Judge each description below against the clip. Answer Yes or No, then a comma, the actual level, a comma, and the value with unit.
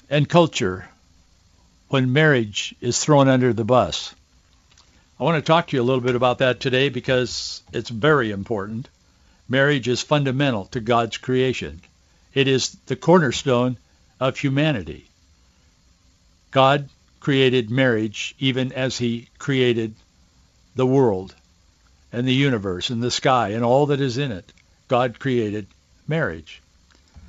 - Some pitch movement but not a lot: No, wide, 7.3 semitones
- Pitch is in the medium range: No, low, 120 Hz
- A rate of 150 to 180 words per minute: No, slow, 135 wpm